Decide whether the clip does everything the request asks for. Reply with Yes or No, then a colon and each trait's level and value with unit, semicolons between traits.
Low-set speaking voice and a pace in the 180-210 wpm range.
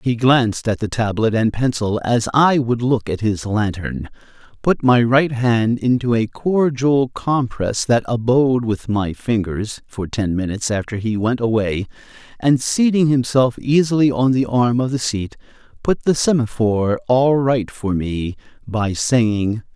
No: low, 120 Hz; average, 160 wpm